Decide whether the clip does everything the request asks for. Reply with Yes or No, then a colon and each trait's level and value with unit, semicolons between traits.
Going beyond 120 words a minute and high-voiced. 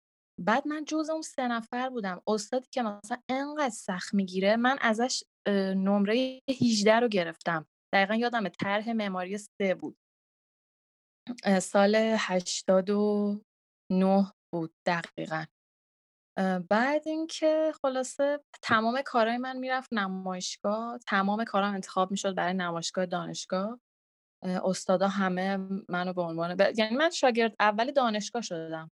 No: average, 115 wpm; high, 205 Hz